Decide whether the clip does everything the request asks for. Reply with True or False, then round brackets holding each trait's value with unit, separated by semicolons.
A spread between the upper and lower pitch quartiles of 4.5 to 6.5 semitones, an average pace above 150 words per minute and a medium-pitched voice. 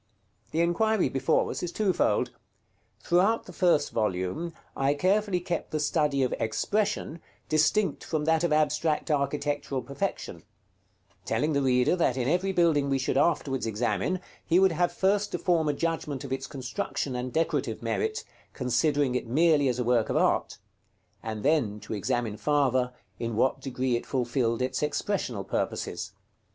True (5.2 semitones; 160 wpm; 145 Hz)